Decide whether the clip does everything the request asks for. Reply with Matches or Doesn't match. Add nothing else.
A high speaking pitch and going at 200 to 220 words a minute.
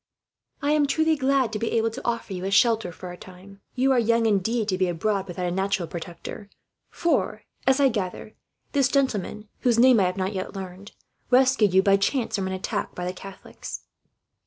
Matches